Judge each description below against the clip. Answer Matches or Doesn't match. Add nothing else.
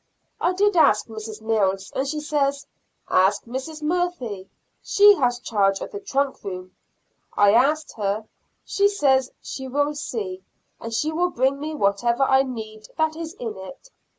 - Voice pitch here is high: Matches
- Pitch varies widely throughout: Matches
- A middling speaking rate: Matches